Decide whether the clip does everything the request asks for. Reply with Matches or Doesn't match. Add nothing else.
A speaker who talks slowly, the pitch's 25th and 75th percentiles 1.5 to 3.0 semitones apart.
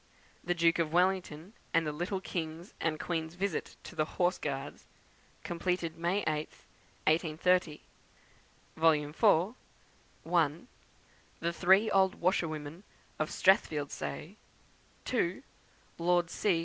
Matches